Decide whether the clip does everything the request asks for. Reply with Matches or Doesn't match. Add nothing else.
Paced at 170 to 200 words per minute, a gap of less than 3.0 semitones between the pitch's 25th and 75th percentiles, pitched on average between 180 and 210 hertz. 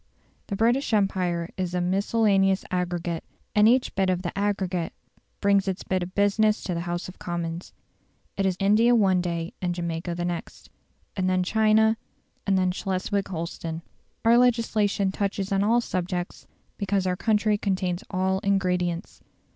Doesn't match